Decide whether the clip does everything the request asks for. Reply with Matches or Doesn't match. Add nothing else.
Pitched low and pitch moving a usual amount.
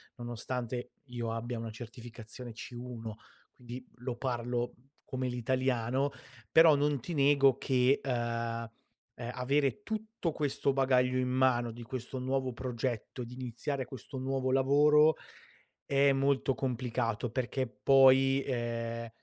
Doesn't match